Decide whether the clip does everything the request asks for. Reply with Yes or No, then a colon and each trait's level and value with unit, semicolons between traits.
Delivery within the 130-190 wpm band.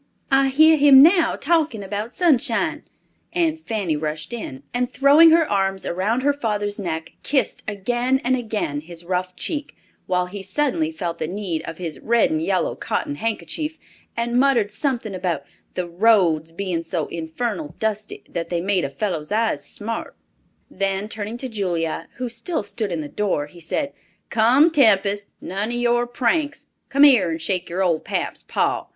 Yes: average, 170 wpm